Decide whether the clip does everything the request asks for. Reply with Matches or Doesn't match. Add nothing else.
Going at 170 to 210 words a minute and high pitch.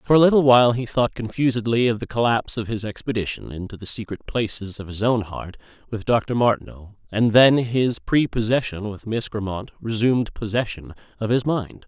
Doesn't match